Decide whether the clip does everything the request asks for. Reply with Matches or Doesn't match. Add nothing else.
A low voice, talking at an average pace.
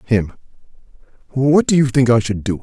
Matches